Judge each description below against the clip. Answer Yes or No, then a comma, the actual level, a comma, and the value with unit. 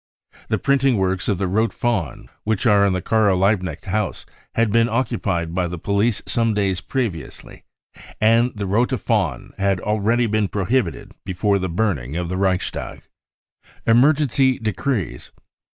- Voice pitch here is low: Yes, low, 105 Hz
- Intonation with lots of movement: No, average, 3.8 semitones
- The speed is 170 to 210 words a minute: No, average, 150 wpm